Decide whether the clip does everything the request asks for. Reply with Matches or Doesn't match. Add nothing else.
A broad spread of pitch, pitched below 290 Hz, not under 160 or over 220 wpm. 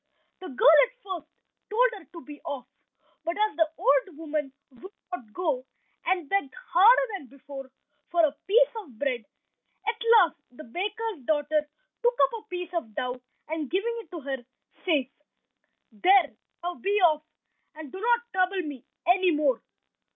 Doesn't match